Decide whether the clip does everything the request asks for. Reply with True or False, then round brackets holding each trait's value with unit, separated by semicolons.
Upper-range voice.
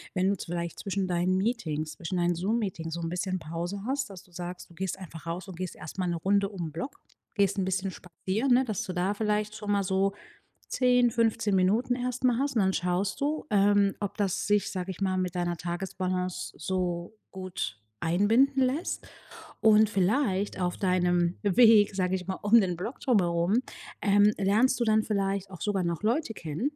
True (195 Hz)